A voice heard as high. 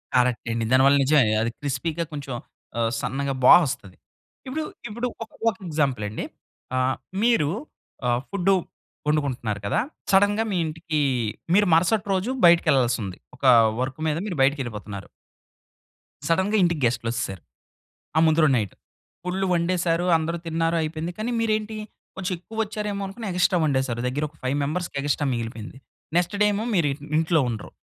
No: medium, 155 Hz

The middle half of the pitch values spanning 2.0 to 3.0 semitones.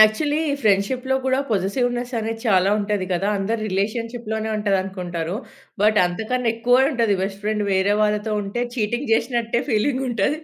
No: average, 3.4 semitones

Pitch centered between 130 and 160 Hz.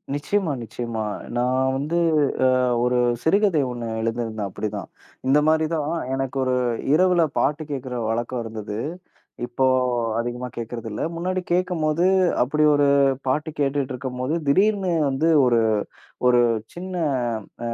Yes: low, 135 Hz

